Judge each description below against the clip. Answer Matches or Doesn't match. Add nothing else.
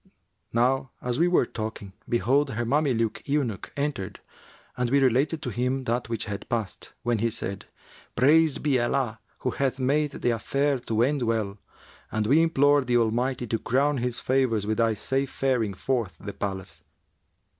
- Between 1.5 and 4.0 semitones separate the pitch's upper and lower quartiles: Matches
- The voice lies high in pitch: Doesn't match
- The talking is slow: Doesn't match